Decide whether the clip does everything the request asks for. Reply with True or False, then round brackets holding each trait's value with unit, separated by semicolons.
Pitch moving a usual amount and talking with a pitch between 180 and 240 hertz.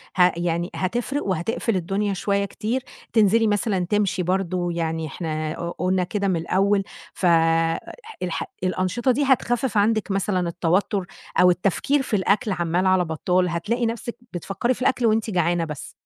True (3.7 semitones; 190 Hz)